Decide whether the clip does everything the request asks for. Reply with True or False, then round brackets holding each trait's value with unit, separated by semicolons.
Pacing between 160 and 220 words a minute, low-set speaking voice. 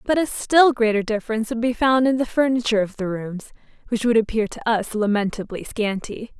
False (195 wpm; 225 Hz)